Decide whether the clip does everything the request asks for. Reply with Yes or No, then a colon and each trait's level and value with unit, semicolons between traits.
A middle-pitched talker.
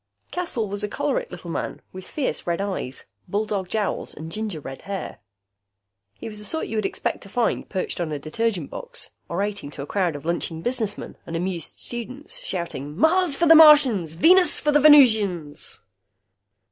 No: high, 205 Hz